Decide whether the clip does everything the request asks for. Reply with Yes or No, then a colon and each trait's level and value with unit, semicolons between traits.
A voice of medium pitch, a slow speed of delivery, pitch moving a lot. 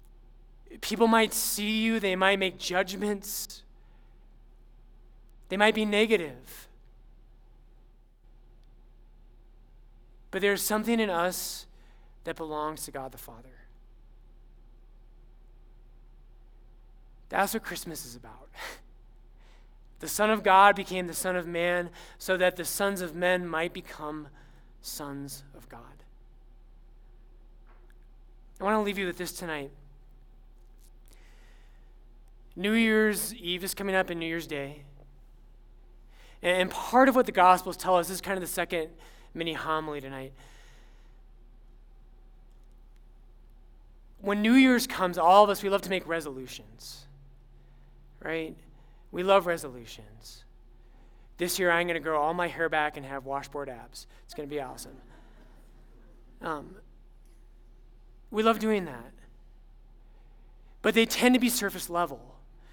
Yes: medium, 145 Hz; slow, 125 wpm; wide, 6.9 semitones